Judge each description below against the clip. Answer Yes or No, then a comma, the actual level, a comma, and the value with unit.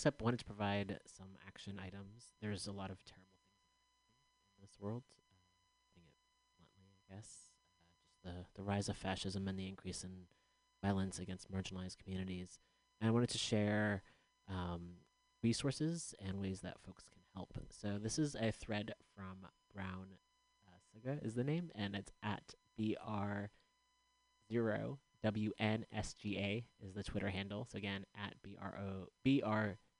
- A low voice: Yes, low, 100 Hz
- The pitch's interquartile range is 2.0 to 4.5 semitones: Yes, average, 2.9 semitones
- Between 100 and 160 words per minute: Yes, average, 140 wpm